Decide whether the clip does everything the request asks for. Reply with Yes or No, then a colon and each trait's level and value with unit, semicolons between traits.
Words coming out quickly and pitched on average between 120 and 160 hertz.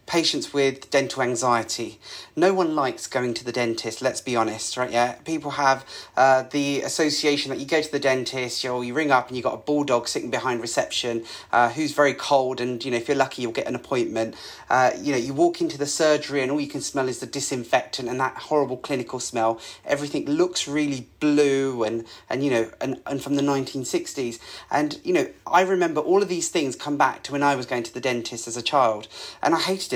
Yes: fast, 230 wpm; low, 135 Hz